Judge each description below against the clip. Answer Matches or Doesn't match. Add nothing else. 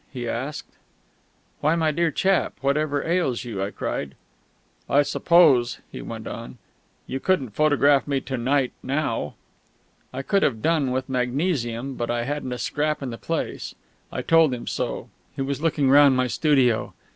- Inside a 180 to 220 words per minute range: Doesn't match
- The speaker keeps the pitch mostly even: Doesn't match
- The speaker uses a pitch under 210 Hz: Matches